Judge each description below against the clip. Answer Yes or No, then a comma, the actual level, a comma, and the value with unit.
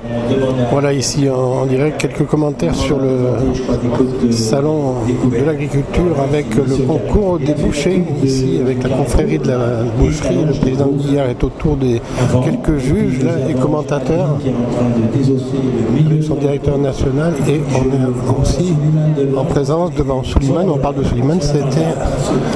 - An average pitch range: No, narrow, 2.3 semitones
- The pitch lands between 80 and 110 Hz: No, low, 135 Hz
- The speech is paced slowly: Yes, slow, 130 wpm